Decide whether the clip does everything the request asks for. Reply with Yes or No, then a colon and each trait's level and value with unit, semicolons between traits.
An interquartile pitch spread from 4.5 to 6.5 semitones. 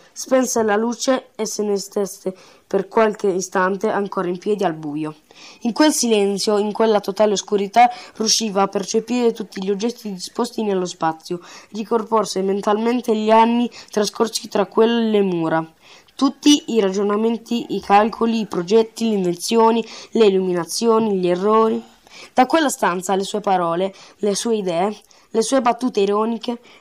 No: average, 2.7 semitones